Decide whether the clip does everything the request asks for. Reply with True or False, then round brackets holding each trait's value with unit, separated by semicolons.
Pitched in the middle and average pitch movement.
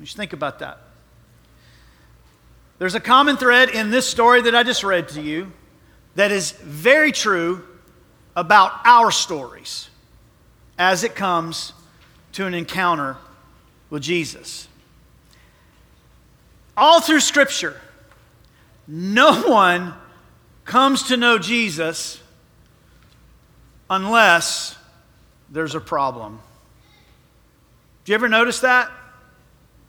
False (175 Hz; 7.8 semitones)